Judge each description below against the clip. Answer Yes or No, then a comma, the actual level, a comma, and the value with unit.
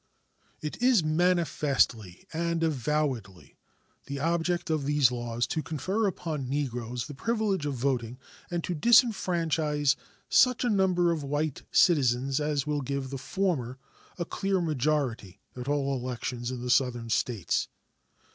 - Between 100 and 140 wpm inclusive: Yes, slow, 135 wpm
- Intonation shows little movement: No, average, 5.1 semitones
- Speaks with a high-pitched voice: No, medium, 145 Hz